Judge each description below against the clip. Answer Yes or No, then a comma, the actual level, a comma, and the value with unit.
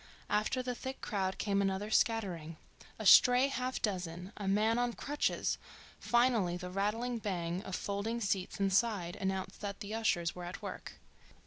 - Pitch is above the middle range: Yes, high, 200 Hz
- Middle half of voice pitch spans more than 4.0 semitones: No, average, 3.7 semitones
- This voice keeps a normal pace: Yes, average, 155 wpm